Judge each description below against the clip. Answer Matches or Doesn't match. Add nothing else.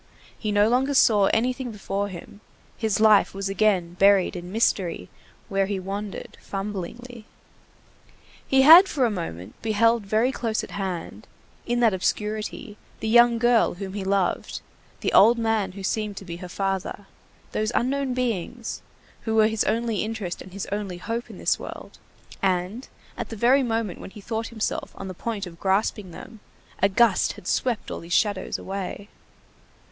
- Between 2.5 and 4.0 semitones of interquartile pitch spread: Matches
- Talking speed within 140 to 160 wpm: Doesn't match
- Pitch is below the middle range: Doesn't match